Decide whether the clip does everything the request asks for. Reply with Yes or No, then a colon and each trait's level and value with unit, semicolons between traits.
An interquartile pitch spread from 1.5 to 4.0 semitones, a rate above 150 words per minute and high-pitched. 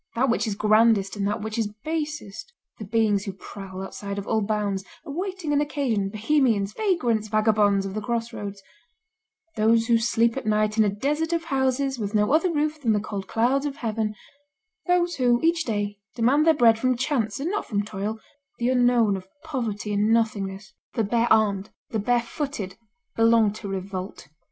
No: average, 4.4 semitones; average, 180 wpm; high, 225 Hz